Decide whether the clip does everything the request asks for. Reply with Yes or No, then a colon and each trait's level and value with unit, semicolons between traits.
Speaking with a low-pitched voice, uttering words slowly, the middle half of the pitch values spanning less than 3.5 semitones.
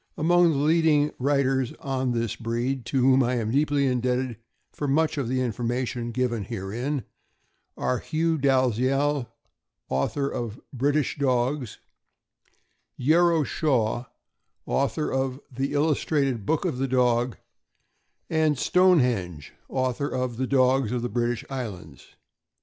Yes: low, 130 Hz; slow, 125 wpm; average, 3.0 semitones